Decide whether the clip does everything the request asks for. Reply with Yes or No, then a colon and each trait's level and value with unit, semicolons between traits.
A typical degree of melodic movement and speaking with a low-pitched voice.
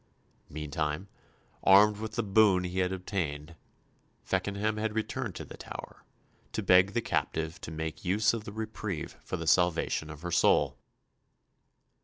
Yes: average, 4.7 semitones; very low, 95 Hz